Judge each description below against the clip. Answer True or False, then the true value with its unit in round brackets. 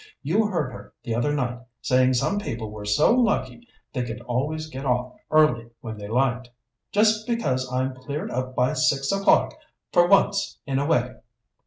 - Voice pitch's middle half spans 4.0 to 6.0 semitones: True (4.3 semitones)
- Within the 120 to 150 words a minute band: False (175 wpm)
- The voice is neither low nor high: False (130 Hz)